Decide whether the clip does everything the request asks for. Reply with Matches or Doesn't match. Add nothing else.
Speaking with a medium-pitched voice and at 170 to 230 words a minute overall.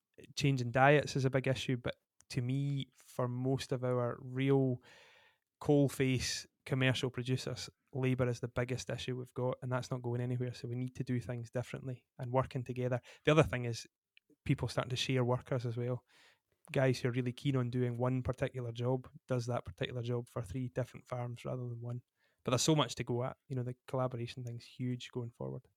Doesn't match